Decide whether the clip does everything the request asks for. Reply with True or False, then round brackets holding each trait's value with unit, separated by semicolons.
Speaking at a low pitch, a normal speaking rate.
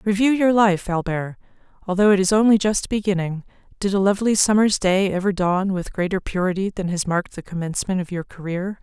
False (190 Hz; 190 wpm)